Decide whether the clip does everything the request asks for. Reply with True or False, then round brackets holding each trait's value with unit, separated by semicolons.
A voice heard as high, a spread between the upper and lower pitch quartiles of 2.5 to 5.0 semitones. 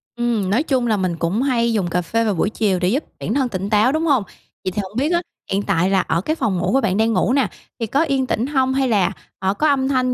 False (225 Hz; 5.5 semitones)